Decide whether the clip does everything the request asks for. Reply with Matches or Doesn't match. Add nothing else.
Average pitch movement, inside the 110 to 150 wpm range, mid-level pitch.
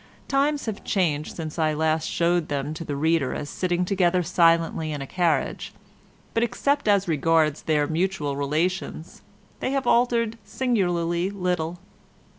Matches